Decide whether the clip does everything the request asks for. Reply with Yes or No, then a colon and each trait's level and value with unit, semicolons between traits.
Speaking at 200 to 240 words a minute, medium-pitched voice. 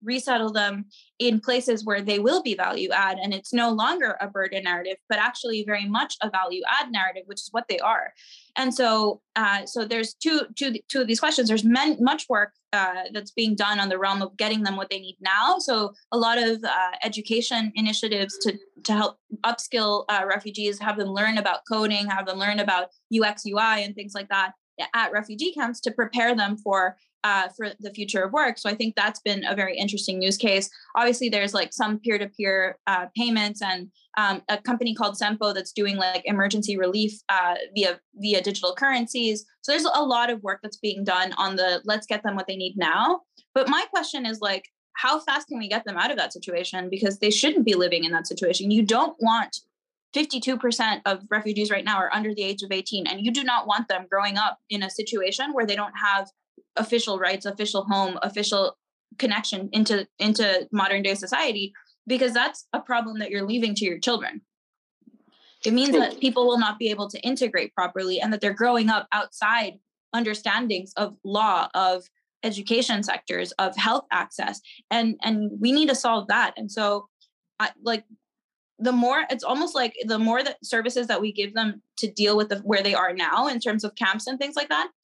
No: fast, 205 wpm; high, 210 Hz